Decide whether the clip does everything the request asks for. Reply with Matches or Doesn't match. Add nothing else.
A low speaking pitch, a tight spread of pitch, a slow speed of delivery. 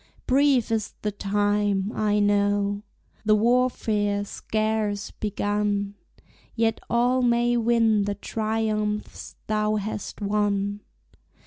Doesn't match